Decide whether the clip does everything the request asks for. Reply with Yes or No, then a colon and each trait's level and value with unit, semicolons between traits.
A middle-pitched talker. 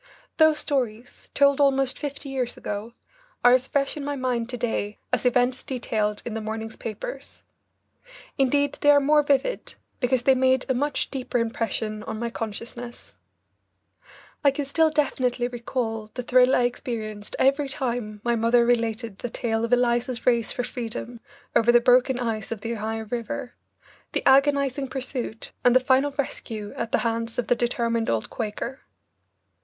No: high, 245 Hz